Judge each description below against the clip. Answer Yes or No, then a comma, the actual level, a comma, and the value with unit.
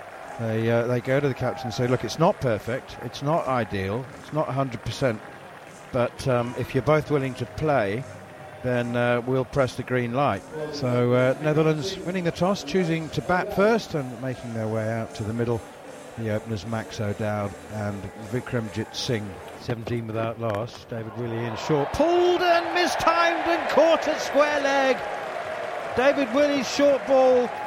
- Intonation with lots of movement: Yes, wide, 6.9 semitones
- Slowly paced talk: No, average, 165 wpm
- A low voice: Yes, low, 130 Hz